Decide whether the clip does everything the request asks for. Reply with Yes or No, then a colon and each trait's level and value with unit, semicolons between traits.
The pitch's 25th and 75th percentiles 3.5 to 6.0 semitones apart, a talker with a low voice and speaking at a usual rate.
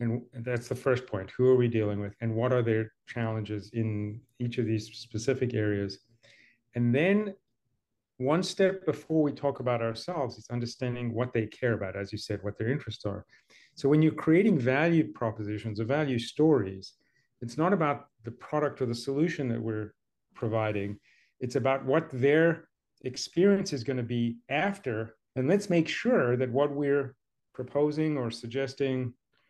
Yes: average, 4.1 semitones; low, 125 Hz; average, 170 wpm